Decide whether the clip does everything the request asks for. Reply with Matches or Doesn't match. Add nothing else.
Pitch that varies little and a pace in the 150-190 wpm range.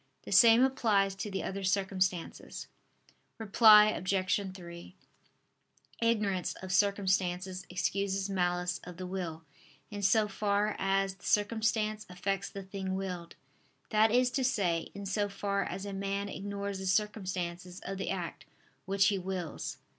Doesn't match